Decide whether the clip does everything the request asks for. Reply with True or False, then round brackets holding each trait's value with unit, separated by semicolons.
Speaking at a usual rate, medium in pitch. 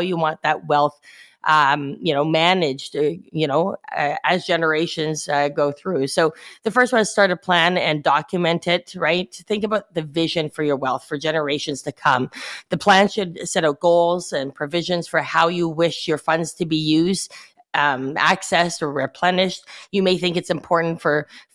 True (185 wpm; 165 Hz)